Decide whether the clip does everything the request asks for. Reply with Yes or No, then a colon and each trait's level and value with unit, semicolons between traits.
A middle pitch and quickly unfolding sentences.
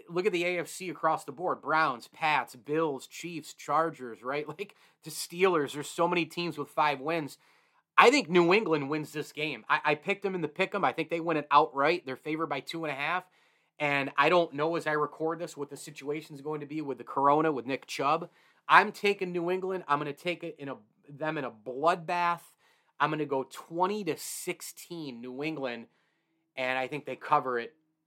Yes: medium, 155 Hz; fast, 215 wpm